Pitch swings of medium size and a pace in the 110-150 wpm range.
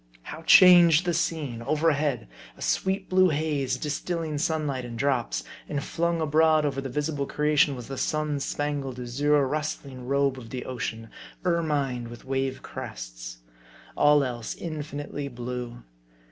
Yes: average, 3.5 semitones; average, 140 wpm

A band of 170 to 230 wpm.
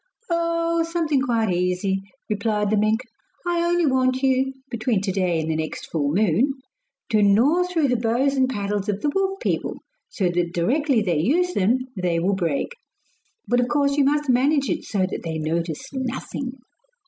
Yes: average, 180 wpm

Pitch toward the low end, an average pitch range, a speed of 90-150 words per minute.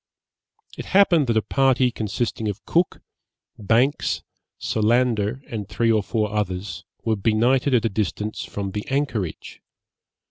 Yes: low, 110 Hz; average, 3.4 semitones; slow, 135 wpm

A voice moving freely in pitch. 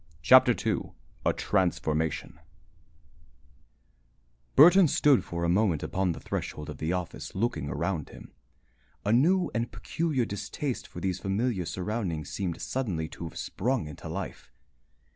Yes: wide, 6.5 semitones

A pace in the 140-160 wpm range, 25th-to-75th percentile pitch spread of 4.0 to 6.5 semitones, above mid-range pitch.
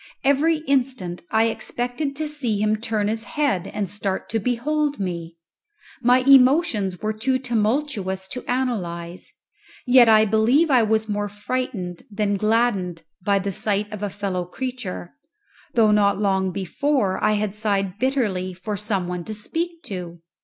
Yes: average, 155 wpm; average, 4.7 semitones; high, 215 Hz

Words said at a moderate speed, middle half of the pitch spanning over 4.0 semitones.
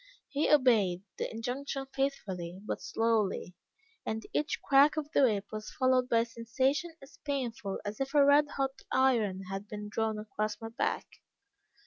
Yes: average, 160 wpm; average, 4.4 semitones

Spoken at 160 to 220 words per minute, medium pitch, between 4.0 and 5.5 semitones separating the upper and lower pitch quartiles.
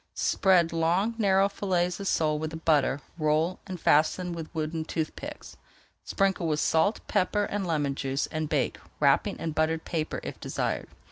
No: average, 165 wpm; medium, 165 Hz; average, 3.3 semitones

